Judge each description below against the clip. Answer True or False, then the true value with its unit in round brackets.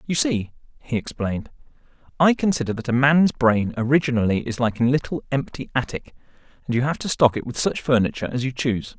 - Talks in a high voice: False (130 Hz)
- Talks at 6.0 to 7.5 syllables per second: True (6.2 syllables/s)